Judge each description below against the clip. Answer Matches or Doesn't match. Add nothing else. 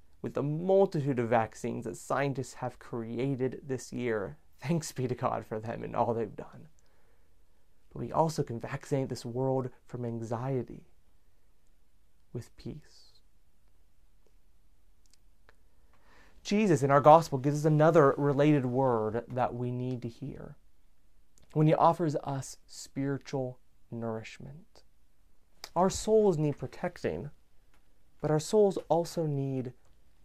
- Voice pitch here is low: Matches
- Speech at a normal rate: Doesn't match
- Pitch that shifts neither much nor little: Doesn't match